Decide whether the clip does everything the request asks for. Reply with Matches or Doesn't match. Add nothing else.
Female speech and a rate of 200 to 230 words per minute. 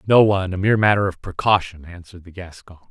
Doesn't match